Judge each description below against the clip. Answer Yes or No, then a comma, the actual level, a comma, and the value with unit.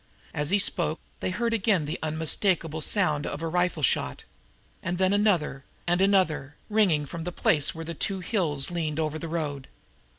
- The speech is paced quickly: No, average, 175 wpm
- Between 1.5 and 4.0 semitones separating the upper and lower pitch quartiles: Yes, average, 3.6 semitones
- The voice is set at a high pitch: No, medium, 165 Hz